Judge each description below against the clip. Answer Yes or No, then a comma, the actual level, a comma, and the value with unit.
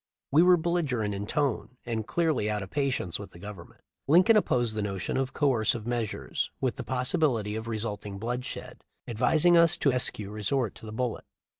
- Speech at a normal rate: Yes, average, 175 wpm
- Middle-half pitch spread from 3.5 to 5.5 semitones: Yes, average, 5.0 semitones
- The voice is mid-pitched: No, low, 120 Hz